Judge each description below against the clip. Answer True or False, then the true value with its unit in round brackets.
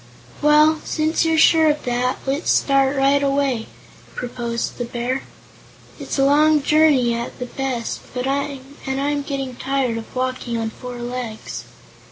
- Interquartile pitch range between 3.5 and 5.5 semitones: False (2.7 semitones)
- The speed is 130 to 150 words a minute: True (145 wpm)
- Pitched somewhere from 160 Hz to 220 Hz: False (270 Hz)